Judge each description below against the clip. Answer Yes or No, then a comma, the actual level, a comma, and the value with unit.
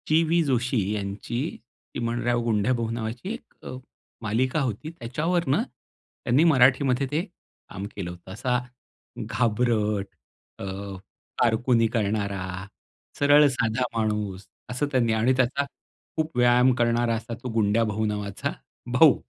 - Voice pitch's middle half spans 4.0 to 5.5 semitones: No, average, 3.3 semitones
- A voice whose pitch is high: No, low, 120 Hz